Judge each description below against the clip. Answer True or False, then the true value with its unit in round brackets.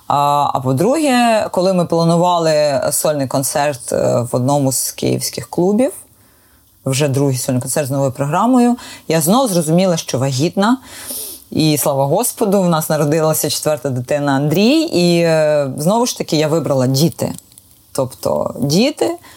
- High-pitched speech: False (155 Hz)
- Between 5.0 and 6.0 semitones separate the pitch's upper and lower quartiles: True (5.3 semitones)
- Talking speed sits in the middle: True (130 wpm)